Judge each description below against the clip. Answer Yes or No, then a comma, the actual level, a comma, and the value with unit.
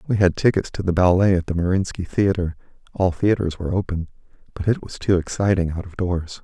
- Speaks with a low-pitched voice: Yes, very low, 90 Hz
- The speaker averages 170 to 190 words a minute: Yes, average, 185 wpm